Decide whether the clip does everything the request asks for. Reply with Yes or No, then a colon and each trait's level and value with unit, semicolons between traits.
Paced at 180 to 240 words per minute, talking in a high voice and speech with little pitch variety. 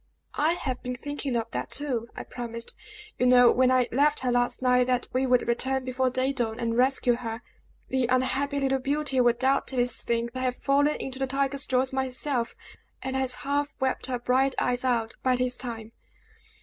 Yes: average, 190 wpm; very high, 255 Hz; narrow, 1.6 semitones